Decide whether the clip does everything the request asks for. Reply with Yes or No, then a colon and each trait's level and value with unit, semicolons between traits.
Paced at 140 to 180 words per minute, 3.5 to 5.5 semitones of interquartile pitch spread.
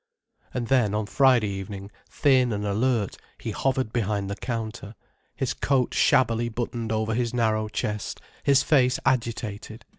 No: average, 145 wpm; average, 3.0 semitones